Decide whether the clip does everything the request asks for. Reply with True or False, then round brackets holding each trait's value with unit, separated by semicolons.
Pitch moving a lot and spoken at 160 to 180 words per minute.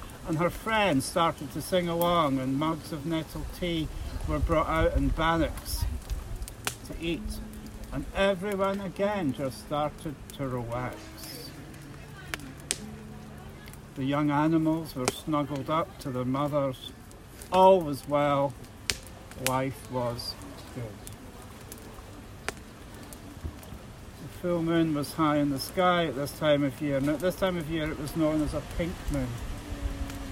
False (6.9 semitones; 135 wpm)